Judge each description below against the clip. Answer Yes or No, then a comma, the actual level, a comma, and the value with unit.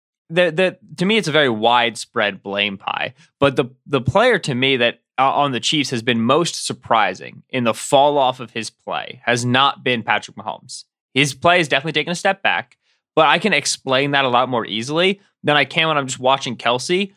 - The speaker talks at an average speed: No, fast, 215 wpm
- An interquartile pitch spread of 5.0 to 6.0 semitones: Yes, average, 5.3 semitones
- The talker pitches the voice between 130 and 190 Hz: Yes, low, 135 Hz